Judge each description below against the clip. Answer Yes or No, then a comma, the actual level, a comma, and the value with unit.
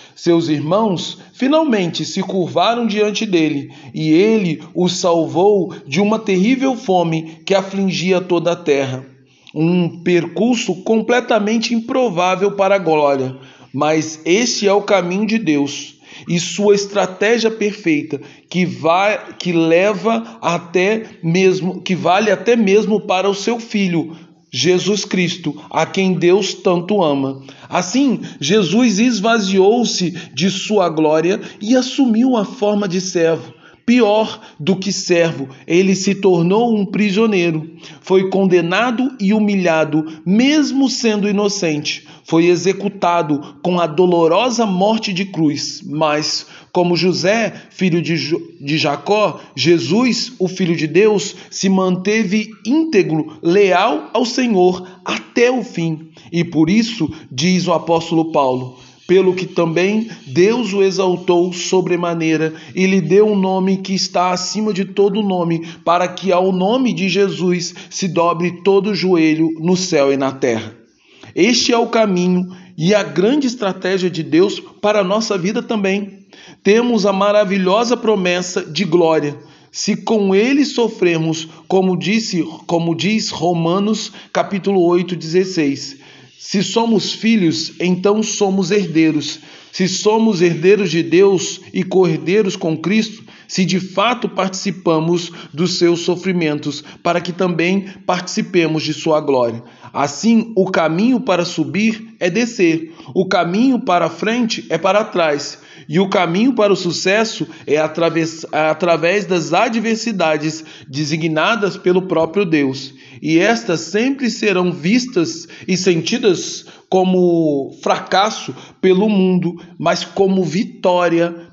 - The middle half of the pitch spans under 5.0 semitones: Yes, average, 4.0 semitones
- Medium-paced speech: Yes, average, 130 wpm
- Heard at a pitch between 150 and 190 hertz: Yes, medium, 185 Hz